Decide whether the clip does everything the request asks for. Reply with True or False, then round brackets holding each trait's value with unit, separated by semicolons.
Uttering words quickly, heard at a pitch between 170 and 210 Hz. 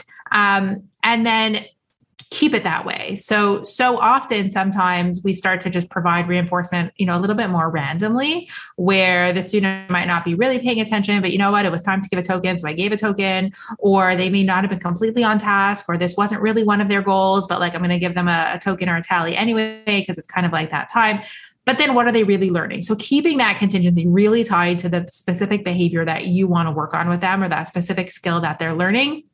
True (245 wpm; 190 Hz)